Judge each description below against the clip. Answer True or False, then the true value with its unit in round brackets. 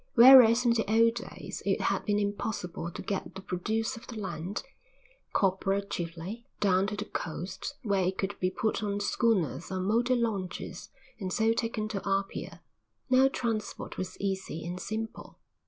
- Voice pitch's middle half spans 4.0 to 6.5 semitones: False (3.2 semitones)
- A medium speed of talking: True (165 wpm)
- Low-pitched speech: False (205 Hz)